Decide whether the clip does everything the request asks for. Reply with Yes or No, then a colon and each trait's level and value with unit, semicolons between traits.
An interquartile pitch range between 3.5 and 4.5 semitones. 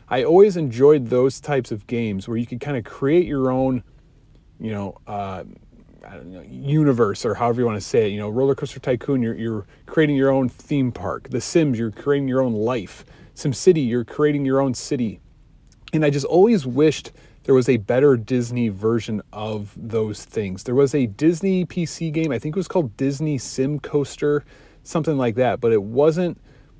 Yes: average, 4.1 semitones